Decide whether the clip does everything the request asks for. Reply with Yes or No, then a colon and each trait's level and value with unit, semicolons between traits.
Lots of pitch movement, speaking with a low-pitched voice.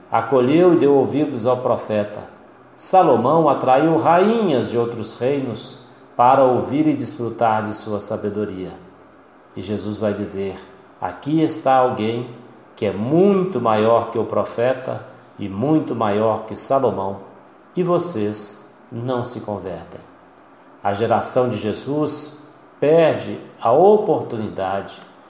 Yes: wide, 5.8 semitones; low, 120 Hz